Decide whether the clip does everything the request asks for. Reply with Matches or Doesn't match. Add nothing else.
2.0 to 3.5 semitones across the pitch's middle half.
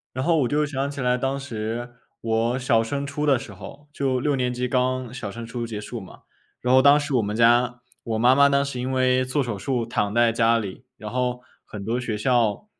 Matches